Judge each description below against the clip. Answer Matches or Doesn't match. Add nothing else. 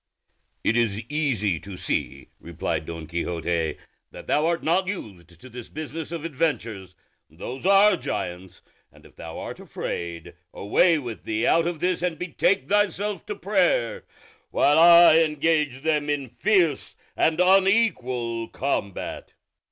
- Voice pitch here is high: Doesn't match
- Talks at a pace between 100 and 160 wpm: Matches